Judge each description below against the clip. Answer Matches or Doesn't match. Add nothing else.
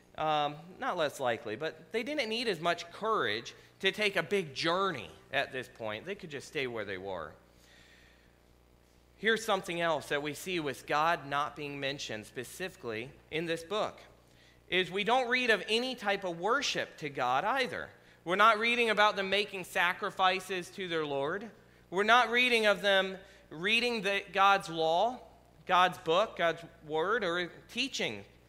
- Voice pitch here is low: Doesn't match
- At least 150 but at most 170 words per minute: Matches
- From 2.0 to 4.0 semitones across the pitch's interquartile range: Doesn't match